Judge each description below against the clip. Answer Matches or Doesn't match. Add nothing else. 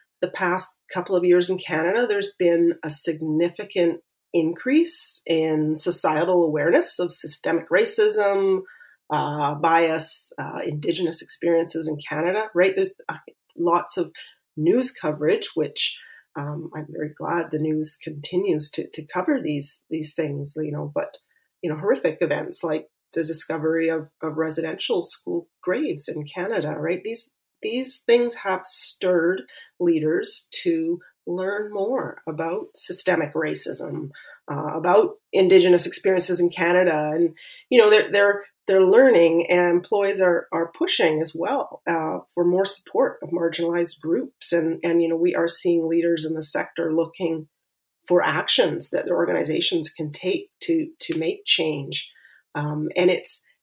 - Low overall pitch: Doesn't match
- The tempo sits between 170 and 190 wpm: Doesn't match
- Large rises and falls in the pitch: Doesn't match